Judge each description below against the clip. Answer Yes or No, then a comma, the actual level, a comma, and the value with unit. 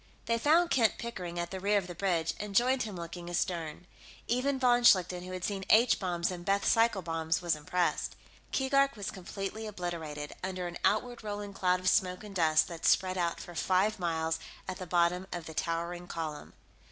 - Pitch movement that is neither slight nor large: Yes, average, 3.4 semitones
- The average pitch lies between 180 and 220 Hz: Yes, medium, 185 Hz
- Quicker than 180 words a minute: Yes, average, 195 wpm